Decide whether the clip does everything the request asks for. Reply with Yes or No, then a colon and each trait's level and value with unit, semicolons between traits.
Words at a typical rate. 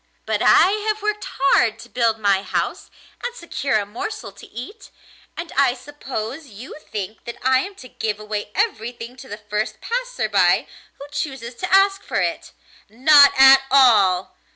Yes: average, 170 wpm